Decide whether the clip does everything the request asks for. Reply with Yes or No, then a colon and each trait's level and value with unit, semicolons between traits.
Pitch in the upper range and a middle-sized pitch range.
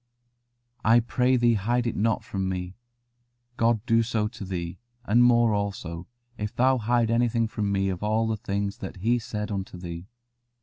No: low, 110 Hz; average, 3.3 semitones